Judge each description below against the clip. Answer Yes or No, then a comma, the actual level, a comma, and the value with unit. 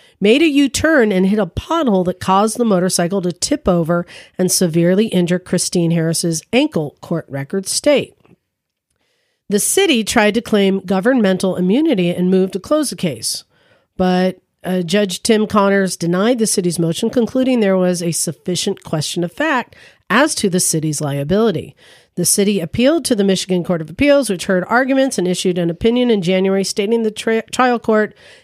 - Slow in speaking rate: No, average, 175 wpm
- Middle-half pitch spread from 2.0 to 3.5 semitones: No, average, 4.2 semitones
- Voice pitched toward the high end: Yes, high, 195 Hz